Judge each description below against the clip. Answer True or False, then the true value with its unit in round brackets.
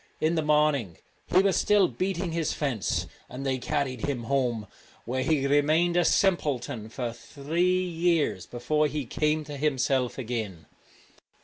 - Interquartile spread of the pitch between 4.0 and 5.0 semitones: True (4.4 semitones)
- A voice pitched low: False (145 Hz)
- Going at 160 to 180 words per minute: False (145 wpm)